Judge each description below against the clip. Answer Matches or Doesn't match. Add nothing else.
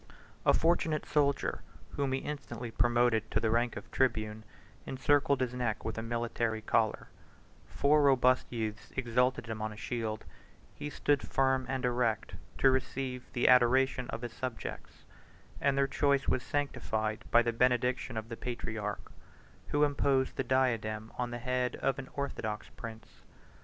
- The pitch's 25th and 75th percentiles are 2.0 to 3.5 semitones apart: Matches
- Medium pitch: Doesn't match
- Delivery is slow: Doesn't match